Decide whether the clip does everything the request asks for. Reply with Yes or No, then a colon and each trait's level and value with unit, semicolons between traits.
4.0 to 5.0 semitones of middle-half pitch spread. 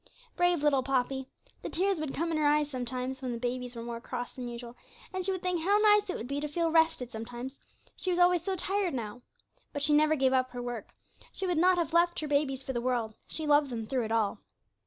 No: wide, 5.5 semitones